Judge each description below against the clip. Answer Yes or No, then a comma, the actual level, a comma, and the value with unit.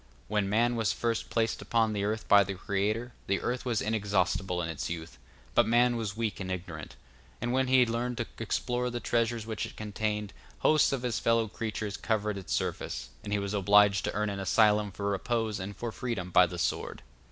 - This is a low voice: Yes, low, 105 Hz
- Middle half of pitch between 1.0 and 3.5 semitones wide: Yes, average, 2.8 semitones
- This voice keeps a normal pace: No, fast, 210 wpm